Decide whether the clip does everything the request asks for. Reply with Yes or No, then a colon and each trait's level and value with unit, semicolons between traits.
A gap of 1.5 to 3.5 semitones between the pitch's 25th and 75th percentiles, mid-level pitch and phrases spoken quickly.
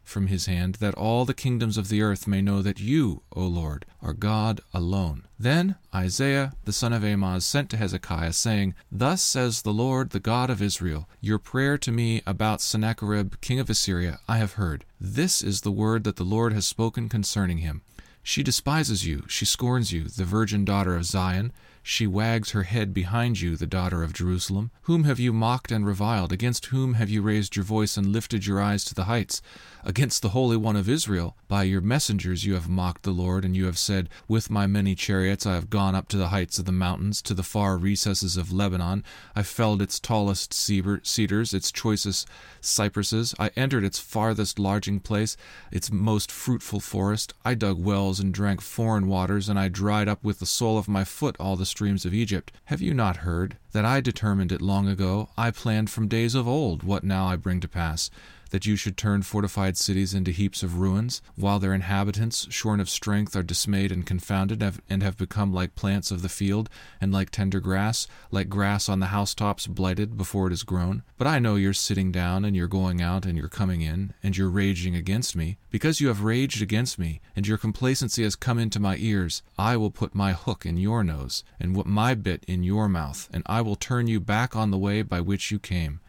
No: average, 2.7 semitones; low, 100 Hz; fast, 210 wpm